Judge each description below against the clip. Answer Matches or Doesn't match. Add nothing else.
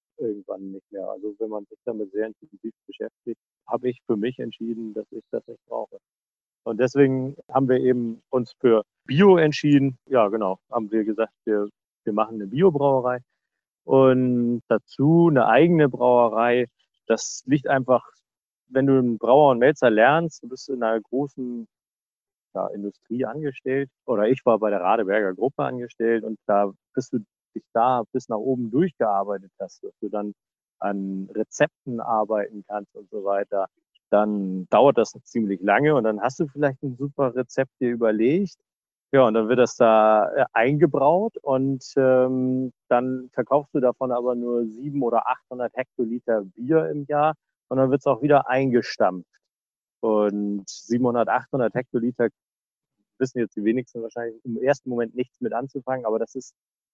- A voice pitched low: Matches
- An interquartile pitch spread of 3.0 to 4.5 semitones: Matches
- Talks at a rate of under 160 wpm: Doesn't match